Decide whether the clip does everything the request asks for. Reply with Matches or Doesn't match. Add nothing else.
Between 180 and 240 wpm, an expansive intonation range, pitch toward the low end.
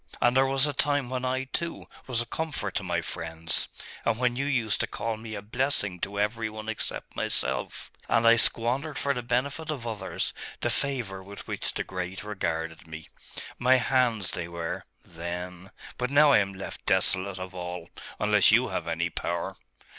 Matches